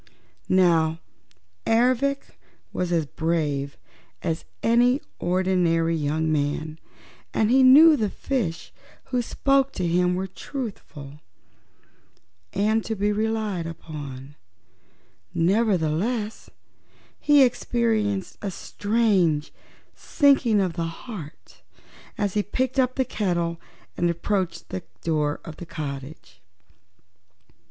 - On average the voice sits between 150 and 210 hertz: Yes, medium, 185 Hz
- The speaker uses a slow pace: Yes, slow, 105 wpm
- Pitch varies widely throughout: Yes, wide, 5.8 semitones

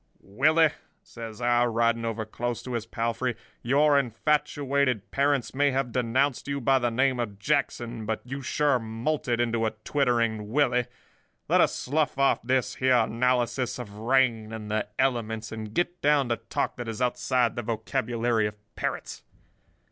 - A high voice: No, low, 120 Hz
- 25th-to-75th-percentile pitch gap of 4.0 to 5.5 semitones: No, average, 3.0 semitones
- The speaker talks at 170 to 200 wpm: No, average, 155 wpm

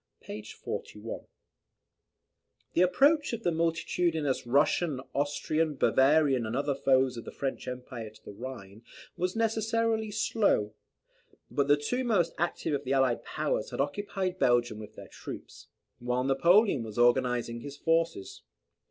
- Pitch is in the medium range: Yes, medium, 145 Hz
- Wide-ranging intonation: Yes, wide, 6.4 semitones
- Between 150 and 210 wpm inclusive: No, average, 140 wpm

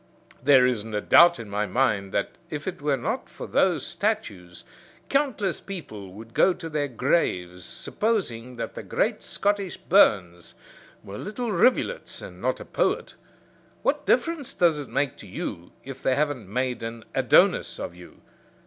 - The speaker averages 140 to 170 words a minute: Yes, average, 160 wpm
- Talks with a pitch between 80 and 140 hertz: Yes, low, 135 Hz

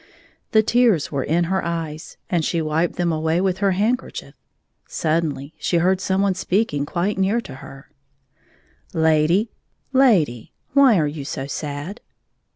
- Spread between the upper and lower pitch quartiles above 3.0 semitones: Yes, average, 4.2 semitones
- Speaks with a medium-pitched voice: Yes, medium, 170 Hz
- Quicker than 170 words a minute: No, average, 155 wpm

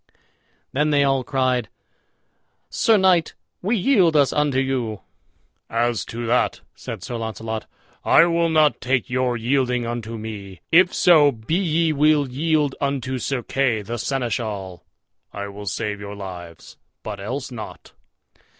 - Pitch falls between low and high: No, low, 130 Hz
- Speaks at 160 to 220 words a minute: No, average, 145 wpm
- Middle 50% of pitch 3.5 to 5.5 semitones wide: Yes, average, 4.9 semitones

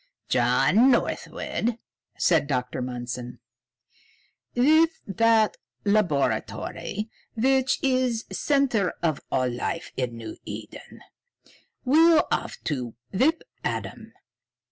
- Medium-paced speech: No, slow, 95 wpm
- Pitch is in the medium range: No, high, 205 Hz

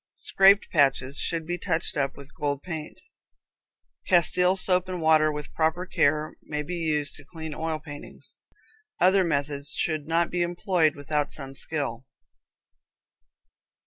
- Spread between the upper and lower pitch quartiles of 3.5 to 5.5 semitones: No, average, 3.1 semitones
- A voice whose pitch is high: No, medium, 155 Hz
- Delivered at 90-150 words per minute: Yes, average, 140 wpm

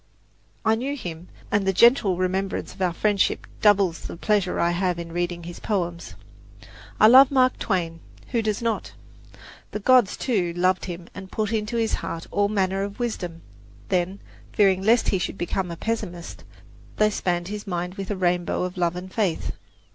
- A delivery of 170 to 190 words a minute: Yes, average, 175 wpm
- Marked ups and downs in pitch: No, average, 3.3 semitones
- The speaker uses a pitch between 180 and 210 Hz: Yes, high, 190 Hz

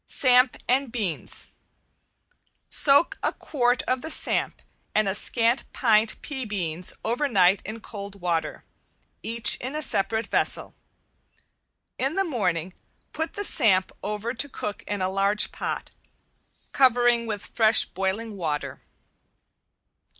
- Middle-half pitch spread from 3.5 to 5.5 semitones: Yes, average, 4.3 semitones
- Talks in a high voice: Yes, high, 225 Hz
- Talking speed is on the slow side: Yes, slow, 130 wpm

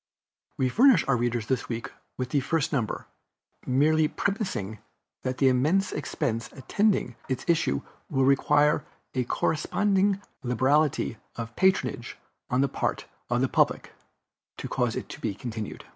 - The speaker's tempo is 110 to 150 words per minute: Yes, average, 145 wpm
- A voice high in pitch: No, low, 135 Hz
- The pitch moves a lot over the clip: No, average, 4.5 semitones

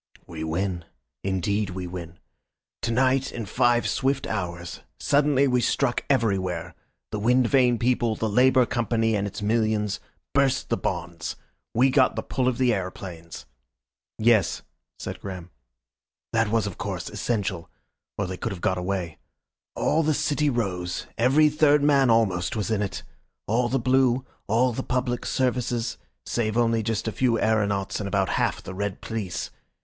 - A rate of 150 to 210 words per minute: Yes, average, 160 wpm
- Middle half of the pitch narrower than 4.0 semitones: No, average, 4.7 semitones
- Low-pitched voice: Yes, low, 115 Hz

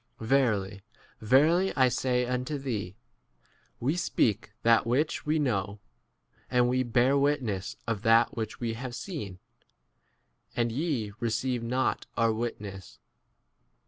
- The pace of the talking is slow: Yes, slow, 130 wpm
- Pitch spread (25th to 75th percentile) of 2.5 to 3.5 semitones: Yes, average, 3.2 semitones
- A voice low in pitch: Yes, low, 120 Hz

